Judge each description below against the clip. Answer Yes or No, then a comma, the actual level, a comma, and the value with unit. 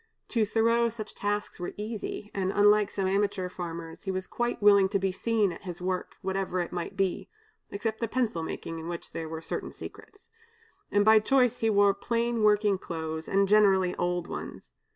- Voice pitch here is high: Yes, high, 200 Hz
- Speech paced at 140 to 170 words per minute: No, average, 190 wpm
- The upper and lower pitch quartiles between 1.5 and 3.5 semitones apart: Yes, average, 3.0 semitones